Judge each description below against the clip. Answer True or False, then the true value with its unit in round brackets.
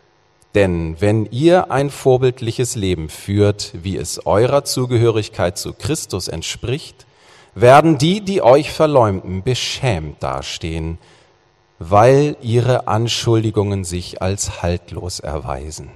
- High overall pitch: False (105 Hz)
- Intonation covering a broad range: True (6.2 semitones)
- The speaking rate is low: True (105 wpm)